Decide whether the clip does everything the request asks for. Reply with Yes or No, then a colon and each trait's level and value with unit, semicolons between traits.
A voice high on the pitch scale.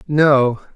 No: medium, 140 Hz